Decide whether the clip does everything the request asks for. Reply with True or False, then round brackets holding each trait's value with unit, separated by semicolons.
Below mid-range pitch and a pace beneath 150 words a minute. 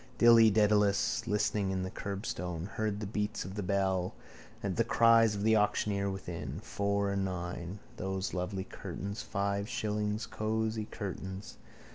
True (100 Hz; 140 wpm)